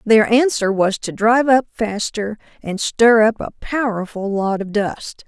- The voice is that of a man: No, female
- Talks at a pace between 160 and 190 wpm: Yes, average, 170 wpm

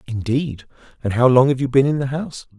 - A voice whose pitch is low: Yes, low, 130 Hz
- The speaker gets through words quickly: Yes, fast, 230 wpm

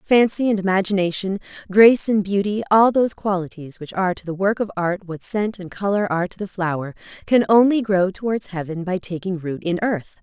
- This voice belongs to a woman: Yes, female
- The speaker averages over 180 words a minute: Yes, average, 200 wpm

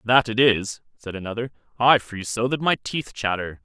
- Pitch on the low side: Yes, low, 115 Hz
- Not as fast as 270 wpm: Yes, average, 200 wpm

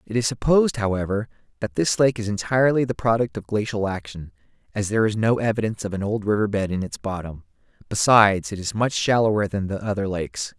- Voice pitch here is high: No, low, 110 Hz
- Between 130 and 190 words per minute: No, fast, 205 wpm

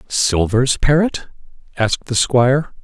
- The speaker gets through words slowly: Yes, slow, 105 wpm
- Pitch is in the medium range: No, low, 130 Hz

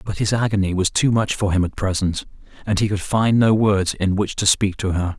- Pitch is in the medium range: No, low, 100 Hz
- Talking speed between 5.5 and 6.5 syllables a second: No, 5.3 syllables/s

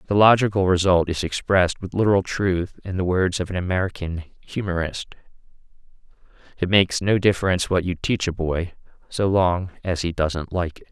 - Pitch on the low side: Yes, very low, 90 Hz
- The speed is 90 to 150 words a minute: No, average, 170 wpm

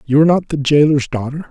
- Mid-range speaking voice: Yes, medium, 145 Hz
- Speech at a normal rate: No, fast, 240 wpm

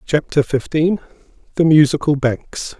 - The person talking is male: Yes, male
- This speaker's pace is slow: Yes, slow, 105 wpm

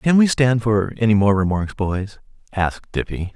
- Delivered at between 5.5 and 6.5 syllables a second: No, 4.7 syllables/s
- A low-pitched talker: Yes, low, 105 Hz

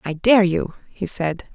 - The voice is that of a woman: Yes, female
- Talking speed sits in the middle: Yes, average, 195 wpm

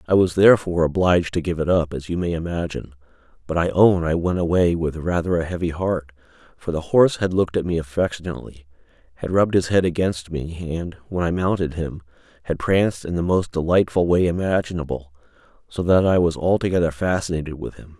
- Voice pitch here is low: Yes, very low, 85 Hz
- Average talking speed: Yes, average, 195 wpm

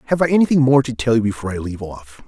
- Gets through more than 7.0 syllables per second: Yes, 7.8 syllables/s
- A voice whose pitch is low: Yes, low, 120 Hz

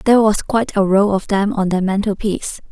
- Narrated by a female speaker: Yes, female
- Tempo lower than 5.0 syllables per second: No, 6.0 syllables/s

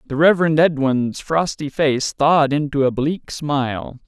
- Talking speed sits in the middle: Yes, average, 145 wpm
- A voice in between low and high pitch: Yes, medium, 145 Hz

